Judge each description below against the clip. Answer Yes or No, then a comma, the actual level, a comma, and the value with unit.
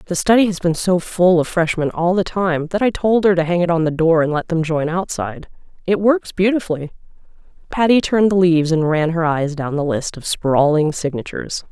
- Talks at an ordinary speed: No, fast, 220 wpm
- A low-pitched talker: No, medium, 170 Hz